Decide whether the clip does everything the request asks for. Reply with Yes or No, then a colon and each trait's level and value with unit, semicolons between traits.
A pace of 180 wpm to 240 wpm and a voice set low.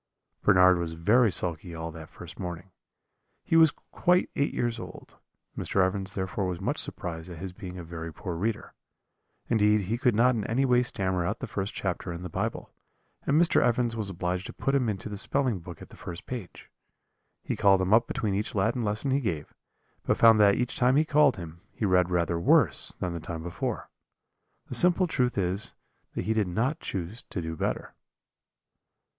Yes: average, 195 wpm; low, 100 Hz